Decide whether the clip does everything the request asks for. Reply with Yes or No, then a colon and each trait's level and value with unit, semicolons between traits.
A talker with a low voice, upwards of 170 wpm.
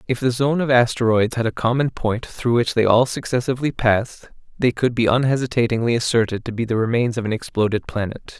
Yes: low, 120 Hz; average, 200 wpm